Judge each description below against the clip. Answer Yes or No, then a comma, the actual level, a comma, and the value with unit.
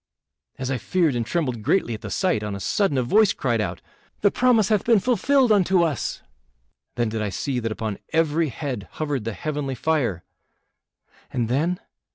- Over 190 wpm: No, average, 185 wpm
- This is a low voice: No, medium, 145 Hz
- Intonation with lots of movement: Yes, wide, 8.2 semitones